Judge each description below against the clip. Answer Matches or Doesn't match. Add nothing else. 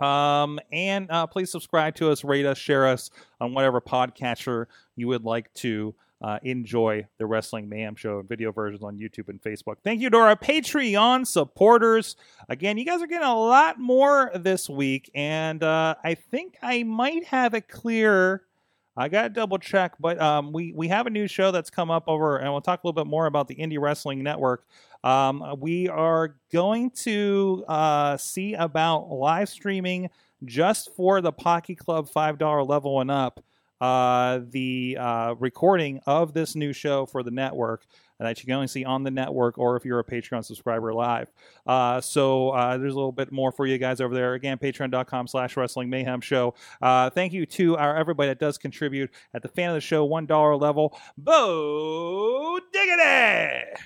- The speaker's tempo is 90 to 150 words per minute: Doesn't match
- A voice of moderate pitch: Matches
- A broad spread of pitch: Matches